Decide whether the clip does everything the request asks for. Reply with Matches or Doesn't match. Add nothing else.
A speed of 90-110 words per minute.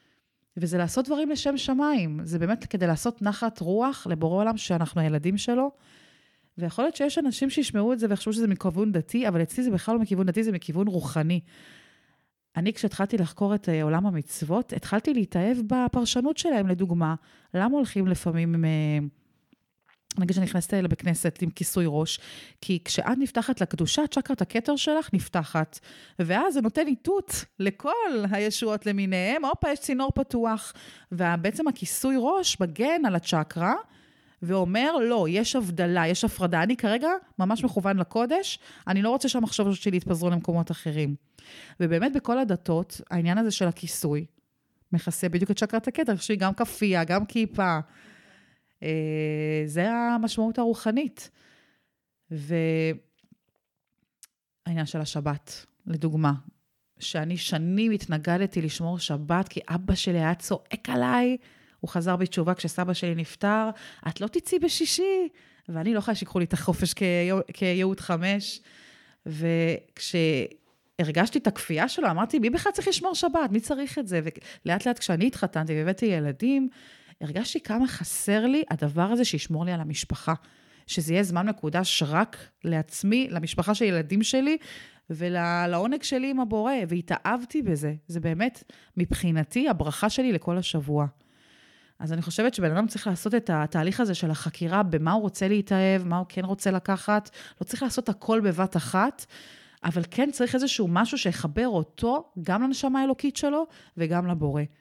Doesn't match